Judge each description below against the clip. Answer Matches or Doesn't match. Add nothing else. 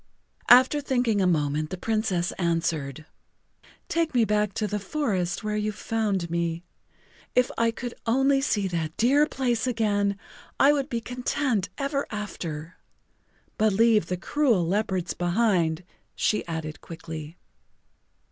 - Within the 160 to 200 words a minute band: Doesn't match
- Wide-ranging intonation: Matches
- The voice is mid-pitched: Doesn't match